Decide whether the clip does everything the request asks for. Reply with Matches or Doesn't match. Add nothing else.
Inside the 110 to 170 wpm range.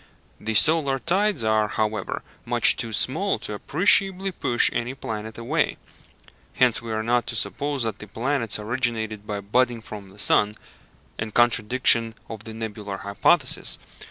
Matches